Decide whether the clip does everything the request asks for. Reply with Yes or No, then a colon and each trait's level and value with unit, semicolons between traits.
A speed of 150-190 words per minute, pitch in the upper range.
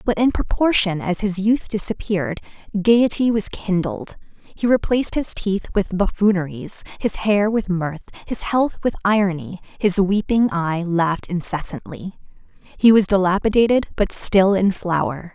No: average, 140 wpm; high, 195 Hz